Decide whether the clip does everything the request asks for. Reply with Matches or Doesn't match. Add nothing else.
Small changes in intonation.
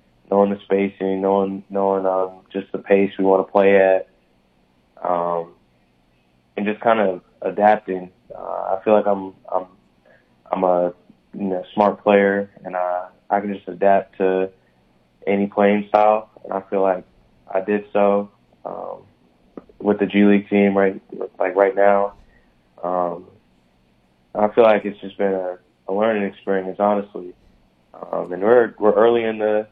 Matches